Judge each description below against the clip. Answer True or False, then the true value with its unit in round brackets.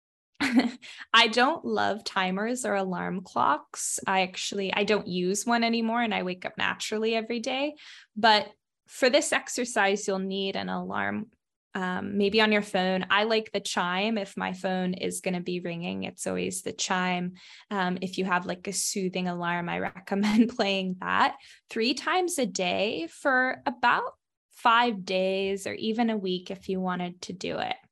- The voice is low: False (195 Hz)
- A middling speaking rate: True (170 wpm)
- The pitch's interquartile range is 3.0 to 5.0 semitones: True (3.7 semitones)